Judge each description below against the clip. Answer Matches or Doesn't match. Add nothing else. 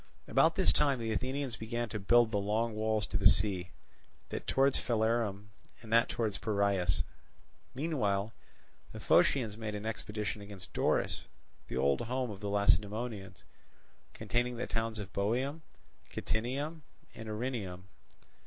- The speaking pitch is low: Matches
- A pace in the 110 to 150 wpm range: Matches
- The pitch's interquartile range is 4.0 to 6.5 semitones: Doesn't match